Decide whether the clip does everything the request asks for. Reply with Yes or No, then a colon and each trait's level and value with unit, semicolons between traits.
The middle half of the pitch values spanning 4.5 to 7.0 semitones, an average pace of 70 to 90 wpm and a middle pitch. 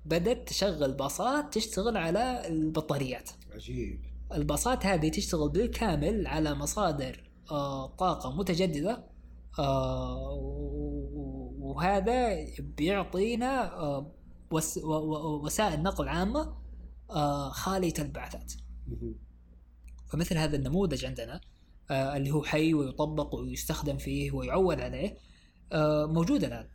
Yes: average, 5.2 semitones; average, 80 wpm; medium, 150 Hz